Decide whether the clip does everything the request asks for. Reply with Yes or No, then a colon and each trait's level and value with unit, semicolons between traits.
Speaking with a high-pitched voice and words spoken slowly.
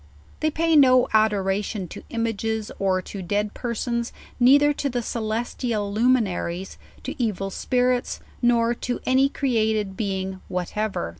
Yes: high, 220 Hz; slow, 130 wpm